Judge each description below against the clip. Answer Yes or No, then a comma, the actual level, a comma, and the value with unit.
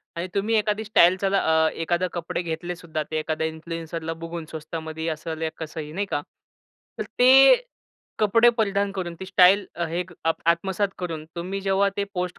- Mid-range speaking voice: Yes, medium, 175 Hz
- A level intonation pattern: No, average, 3.4 semitones